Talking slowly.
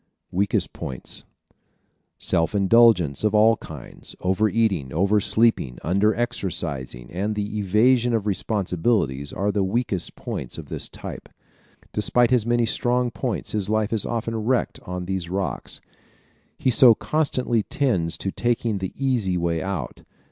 No: average, 145 wpm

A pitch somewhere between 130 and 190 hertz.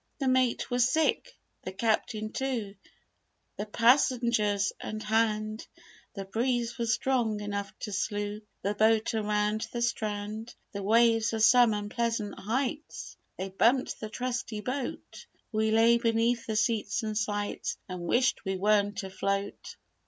No: high, 220 Hz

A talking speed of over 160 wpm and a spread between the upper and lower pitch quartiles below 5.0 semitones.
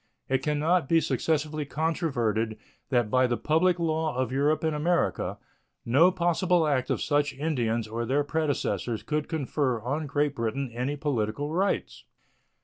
No: average, 150 wpm; average, 4.0 semitones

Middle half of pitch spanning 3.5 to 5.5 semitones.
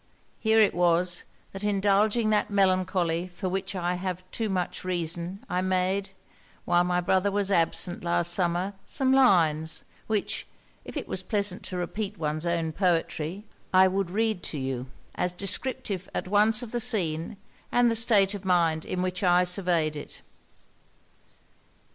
No: average, 2.7 semitones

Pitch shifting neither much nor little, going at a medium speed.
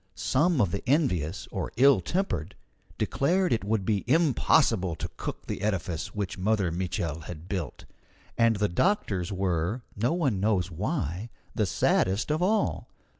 No: wide, 6.9 semitones; average, 150 wpm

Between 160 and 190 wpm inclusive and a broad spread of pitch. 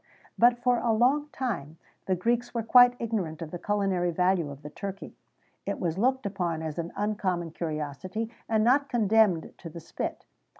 Yes: average, 185 wpm; wide, 5.7 semitones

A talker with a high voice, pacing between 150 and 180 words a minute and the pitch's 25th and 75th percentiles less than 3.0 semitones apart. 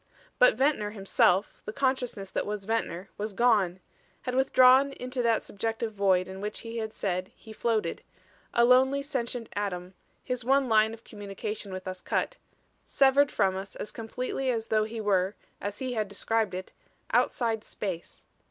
No: high, 220 Hz; average, 165 wpm; average, 4.0 semitones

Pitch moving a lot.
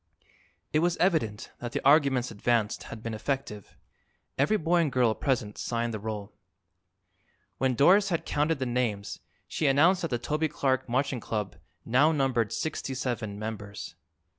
No: average, 5.0 semitones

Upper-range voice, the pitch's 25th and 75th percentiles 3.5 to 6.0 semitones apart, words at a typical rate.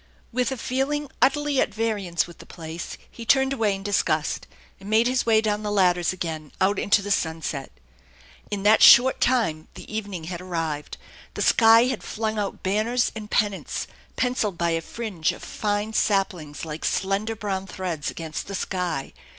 Yes: high, 205 Hz; average, 4.6 semitones; average, 175 wpm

